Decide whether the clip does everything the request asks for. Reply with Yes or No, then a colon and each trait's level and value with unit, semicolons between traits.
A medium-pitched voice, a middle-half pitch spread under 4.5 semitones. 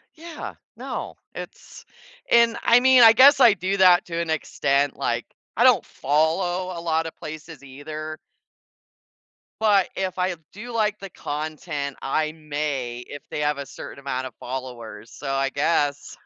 No: medium, 155 Hz; average, 5.2 semitones